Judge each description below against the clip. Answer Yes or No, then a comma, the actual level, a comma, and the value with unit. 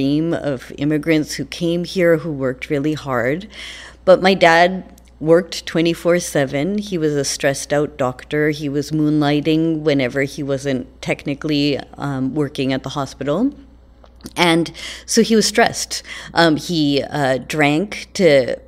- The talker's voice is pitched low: No, medium, 150 Hz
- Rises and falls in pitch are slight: No, average, 3.2 semitones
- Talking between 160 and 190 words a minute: No, average, 140 wpm